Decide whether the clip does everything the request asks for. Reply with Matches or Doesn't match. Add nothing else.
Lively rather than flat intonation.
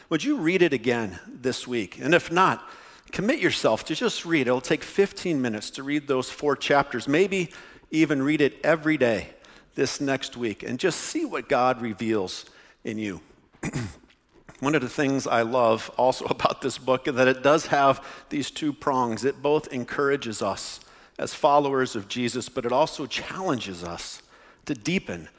Doesn't match